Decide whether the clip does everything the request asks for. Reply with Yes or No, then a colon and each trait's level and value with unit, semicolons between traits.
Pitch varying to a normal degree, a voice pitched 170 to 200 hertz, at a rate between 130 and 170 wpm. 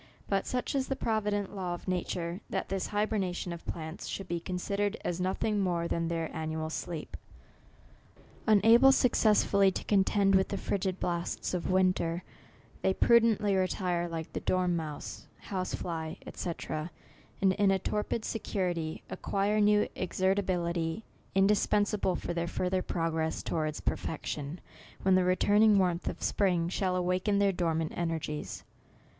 Yes: average, 3.0 semitones; medium, 185 Hz; average, 145 wpm